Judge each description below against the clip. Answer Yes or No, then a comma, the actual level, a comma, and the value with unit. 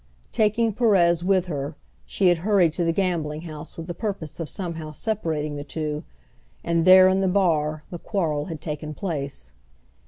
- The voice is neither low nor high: Yes, medium, 170 Hz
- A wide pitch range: No, average, 3.7 semitones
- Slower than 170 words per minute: No, average, 175 wpm